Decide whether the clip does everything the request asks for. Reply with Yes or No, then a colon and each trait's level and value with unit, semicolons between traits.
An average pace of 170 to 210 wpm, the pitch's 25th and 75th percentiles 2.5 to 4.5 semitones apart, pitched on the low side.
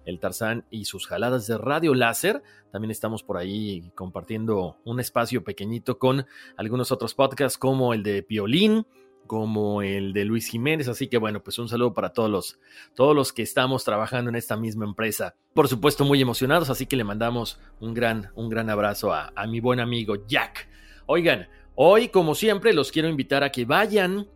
Yes: average, 185 wpm; average, 3.6 semitones; low, 120 Hz